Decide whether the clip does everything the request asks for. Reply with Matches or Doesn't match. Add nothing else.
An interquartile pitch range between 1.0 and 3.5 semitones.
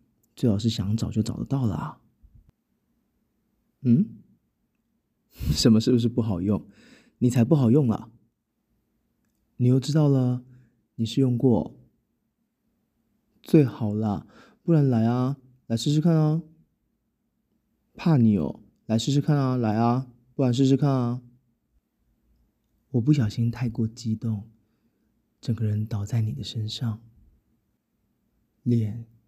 Matches